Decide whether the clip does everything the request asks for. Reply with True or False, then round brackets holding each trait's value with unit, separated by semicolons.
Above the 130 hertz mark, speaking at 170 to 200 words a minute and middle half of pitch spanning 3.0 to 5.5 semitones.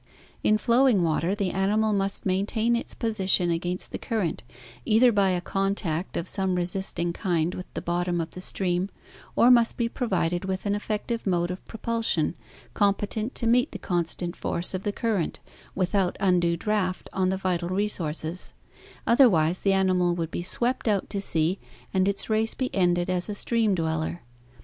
True (190 Hz; 175 wpm; 3.3 semitones)